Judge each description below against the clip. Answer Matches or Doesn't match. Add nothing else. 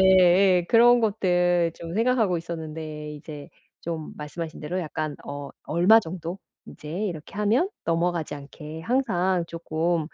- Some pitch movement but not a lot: Matches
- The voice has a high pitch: Doesn't match